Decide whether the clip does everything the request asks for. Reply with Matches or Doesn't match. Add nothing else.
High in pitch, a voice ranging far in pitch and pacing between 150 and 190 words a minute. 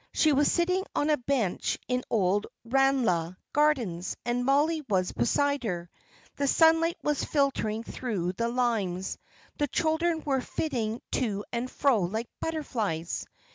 Doesn't match